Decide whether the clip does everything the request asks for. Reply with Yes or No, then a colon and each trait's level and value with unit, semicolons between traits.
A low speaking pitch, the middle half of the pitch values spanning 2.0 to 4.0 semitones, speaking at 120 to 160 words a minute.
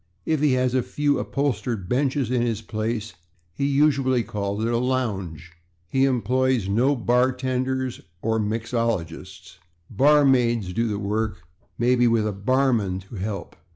Yes: low, 120 Hz; average, 3.6 semitones; average, 140 wpm